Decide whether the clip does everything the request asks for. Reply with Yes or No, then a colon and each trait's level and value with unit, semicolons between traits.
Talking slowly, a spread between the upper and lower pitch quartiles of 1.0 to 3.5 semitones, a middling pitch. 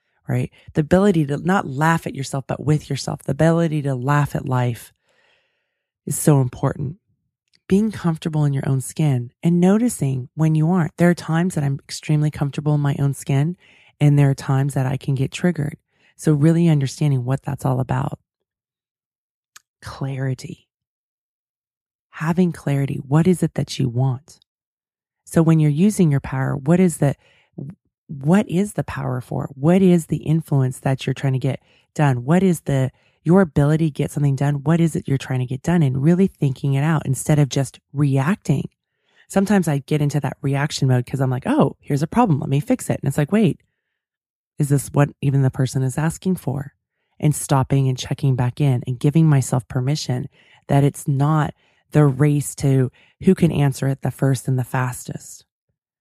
No: average, 185 wpm; average, 3.1 semitones; medium, 145 Hz